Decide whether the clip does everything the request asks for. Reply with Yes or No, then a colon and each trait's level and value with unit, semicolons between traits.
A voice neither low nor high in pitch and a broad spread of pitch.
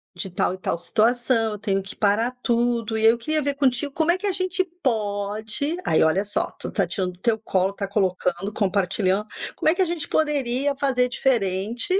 No: high, 225 Hz; wide, 5.7 semitones